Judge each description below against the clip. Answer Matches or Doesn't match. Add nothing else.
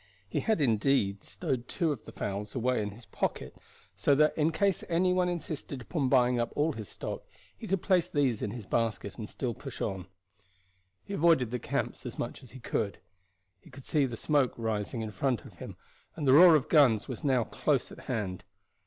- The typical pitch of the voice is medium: Doesn't match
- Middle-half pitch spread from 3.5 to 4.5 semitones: Doesn't match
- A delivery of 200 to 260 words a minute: Matches